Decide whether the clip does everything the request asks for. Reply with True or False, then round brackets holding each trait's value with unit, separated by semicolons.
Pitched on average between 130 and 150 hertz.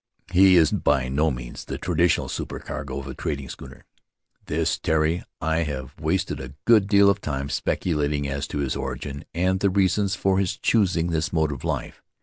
False (80 Hz)